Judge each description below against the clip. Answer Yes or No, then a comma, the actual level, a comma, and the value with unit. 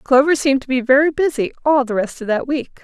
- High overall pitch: Yes, very high, 270 Hz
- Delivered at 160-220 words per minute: No, fast, 255 wpm